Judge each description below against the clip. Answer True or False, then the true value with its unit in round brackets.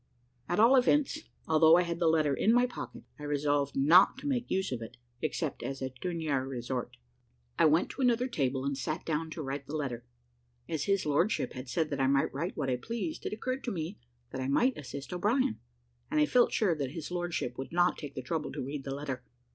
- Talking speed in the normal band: False (225 wpm)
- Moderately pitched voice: True (155 Hz)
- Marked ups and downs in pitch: True (6.3 semitones)